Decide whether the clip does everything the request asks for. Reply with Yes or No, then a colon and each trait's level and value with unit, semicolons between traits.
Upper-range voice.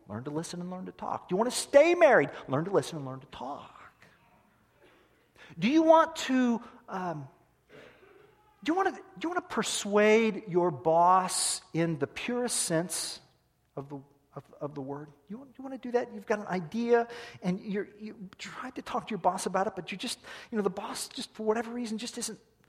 Yes: high, 210 Hz